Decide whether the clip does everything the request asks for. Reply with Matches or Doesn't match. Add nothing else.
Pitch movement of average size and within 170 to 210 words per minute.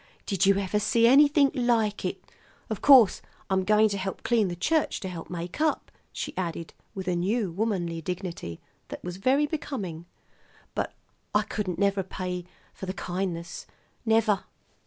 Doesn't match